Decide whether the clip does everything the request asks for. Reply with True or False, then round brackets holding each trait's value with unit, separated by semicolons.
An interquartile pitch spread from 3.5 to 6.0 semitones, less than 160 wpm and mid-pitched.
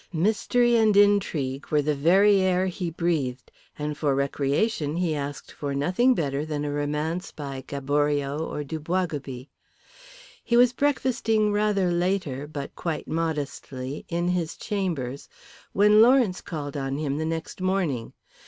True (5.2 semitones; 145 wpm; 160 Hz)